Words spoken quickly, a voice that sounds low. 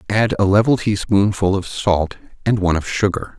No: average, 175 wpm; low, 100 Hz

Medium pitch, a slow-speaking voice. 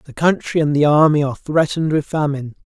No: medium, 150 Hz; average, 200 wpm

